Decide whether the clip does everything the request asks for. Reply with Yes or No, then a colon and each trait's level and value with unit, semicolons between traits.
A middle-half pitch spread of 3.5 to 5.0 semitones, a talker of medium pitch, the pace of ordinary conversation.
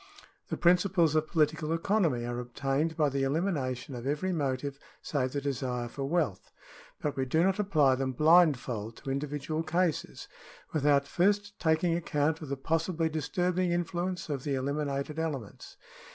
Yes: average, 3.8 semitones; medium, 150 Hz; average, 155 wpm